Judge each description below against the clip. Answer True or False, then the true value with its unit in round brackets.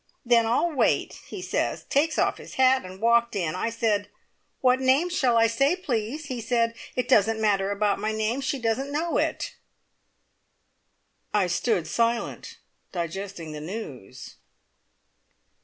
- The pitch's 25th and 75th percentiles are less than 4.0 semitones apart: False (4.3 semitones)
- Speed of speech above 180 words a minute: False (145 wpm)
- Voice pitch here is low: False (230 Hz)